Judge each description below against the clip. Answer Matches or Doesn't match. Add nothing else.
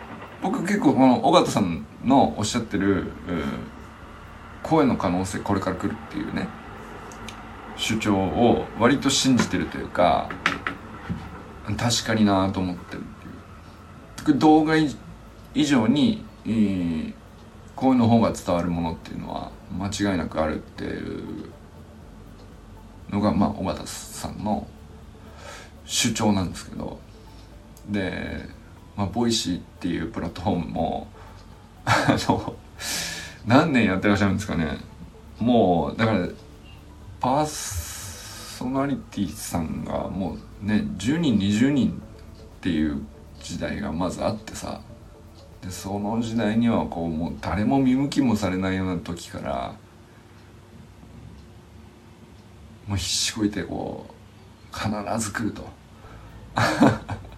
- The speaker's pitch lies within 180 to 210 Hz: Doesn't match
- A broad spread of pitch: Doesn't match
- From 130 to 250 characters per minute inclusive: Matches